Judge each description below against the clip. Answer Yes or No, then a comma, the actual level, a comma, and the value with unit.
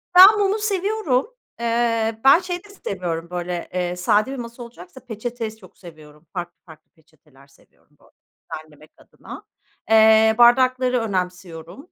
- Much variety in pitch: Yes, wide, 6.6 semitones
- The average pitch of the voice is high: Yes, high, 220 Hz